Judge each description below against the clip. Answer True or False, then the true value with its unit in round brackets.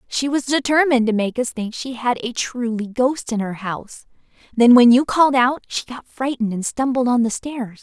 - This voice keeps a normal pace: False (215 wpm)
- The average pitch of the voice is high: True (245 Hz)